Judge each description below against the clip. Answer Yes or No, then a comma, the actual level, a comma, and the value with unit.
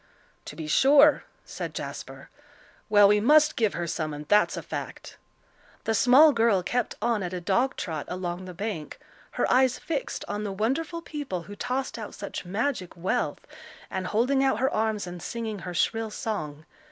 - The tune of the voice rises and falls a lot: Yes, wide, 5.9 semitones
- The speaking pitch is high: Yes, high, 210 Hz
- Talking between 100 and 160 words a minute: No, average, 175 wpm